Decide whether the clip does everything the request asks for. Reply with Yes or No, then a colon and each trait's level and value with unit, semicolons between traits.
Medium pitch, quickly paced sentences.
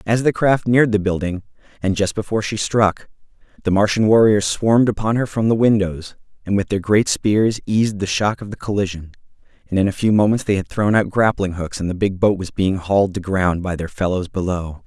No: low, 100 Hz; fast, 220 wpm